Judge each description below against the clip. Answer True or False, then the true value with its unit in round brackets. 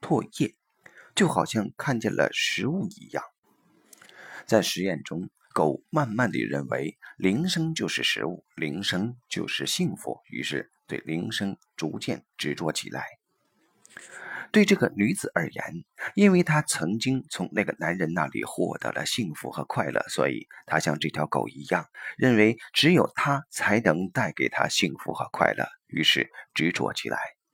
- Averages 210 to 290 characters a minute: True (220 characters per minute)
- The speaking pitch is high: False (110 Hz)